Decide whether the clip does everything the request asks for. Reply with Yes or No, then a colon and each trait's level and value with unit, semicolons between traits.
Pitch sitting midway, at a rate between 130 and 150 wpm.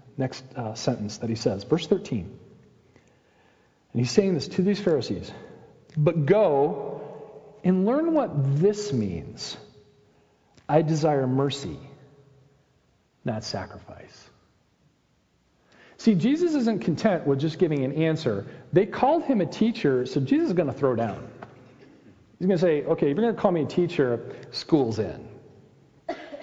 Yes: medium, 155 Hz; average, 145 wpm